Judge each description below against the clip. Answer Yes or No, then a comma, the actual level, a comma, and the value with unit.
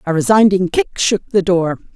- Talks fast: No, average, 185 wpm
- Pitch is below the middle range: No, high, 190 Hz